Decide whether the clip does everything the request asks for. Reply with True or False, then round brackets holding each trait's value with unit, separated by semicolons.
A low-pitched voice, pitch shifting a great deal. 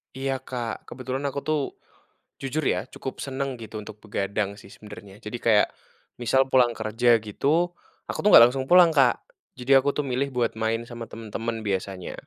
False (120 Hz; 3.8 semitones)